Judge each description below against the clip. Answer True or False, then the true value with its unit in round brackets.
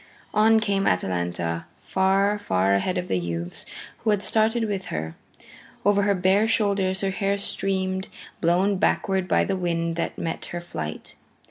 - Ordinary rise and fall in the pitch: True (3.4 semitones)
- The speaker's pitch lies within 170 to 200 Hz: True (190 Hz)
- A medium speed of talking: True (155 wpm)